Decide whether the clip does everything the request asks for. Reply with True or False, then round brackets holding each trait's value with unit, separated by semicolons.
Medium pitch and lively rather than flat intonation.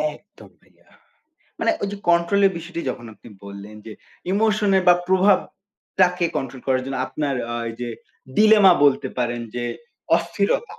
True (170 Hz; 7.5 semitones)